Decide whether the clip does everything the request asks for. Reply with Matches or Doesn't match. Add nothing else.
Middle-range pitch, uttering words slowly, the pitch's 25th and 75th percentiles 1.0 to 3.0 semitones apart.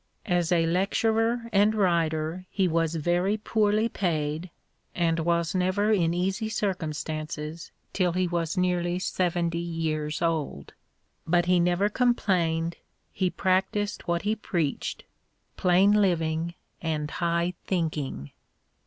Matches